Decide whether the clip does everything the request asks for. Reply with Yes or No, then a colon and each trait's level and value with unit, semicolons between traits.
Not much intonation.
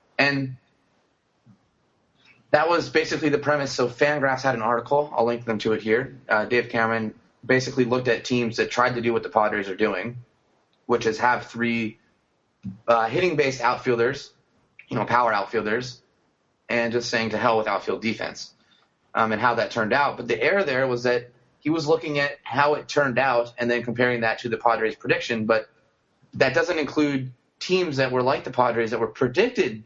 No: average, 3.0 semitones